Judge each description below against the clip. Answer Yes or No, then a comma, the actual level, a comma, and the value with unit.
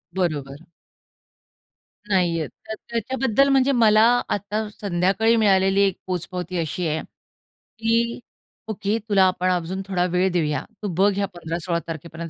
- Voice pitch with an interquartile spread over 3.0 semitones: Yes, average, 3.9 semitones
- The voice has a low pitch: No, high, 190 Hz